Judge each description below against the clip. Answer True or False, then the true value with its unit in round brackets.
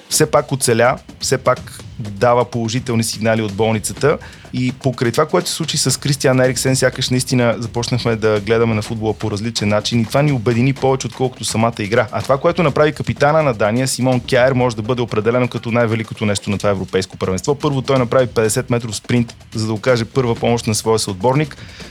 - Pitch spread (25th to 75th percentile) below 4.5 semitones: True (2.8 semitones)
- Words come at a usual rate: False (195 wpm)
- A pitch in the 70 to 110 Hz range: False (120 Hz)